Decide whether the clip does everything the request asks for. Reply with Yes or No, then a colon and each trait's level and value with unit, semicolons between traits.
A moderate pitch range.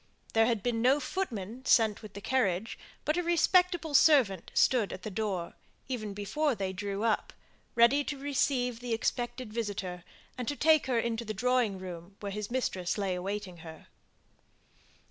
Yes: average, 4.6 semitones